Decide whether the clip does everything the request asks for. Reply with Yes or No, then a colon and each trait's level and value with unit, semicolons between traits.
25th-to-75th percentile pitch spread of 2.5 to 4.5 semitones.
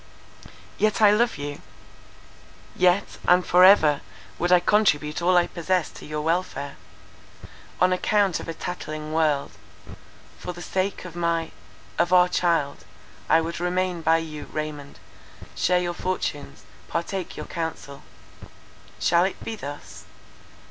Yes: average, 3.1 semitones